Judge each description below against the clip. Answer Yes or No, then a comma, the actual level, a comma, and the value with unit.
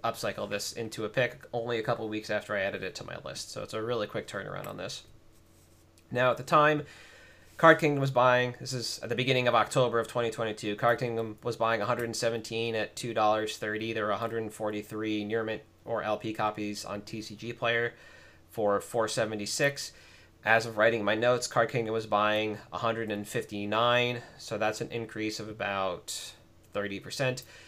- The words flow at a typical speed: Yes, average, 170 wpm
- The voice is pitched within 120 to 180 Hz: No, low, 110 Hz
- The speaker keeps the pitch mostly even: Yes, narrow, 2.0 semitones